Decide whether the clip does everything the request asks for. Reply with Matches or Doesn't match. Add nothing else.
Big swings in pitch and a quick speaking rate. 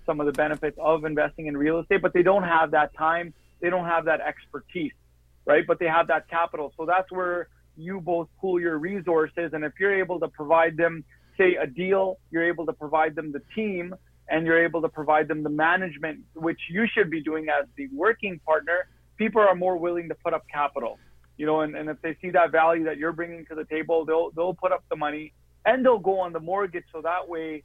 Doesn't match